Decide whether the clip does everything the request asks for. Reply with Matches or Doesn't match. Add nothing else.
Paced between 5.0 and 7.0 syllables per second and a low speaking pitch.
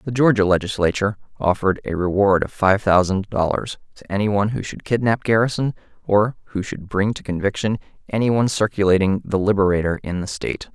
Matches